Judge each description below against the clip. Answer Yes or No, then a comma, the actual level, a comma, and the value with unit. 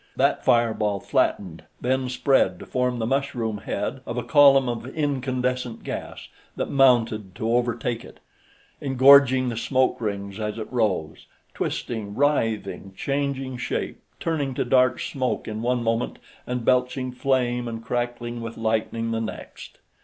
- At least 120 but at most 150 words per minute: Yes, average, 145 wpm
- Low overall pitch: Yes, low, 120 Hz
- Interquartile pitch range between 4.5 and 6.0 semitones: No, narrow, 2.6 semitones